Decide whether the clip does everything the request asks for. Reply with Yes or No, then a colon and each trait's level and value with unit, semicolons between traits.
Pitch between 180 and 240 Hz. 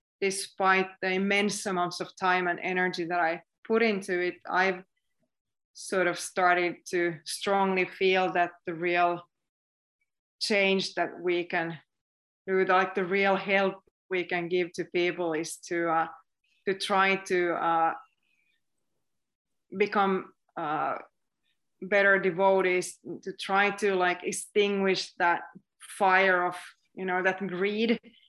Yes: medium, 185 Hz